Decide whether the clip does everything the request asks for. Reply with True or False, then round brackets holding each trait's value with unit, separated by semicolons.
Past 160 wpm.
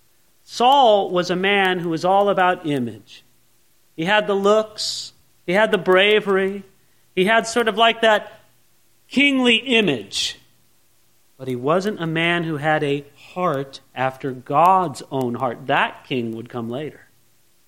False (145 wpm)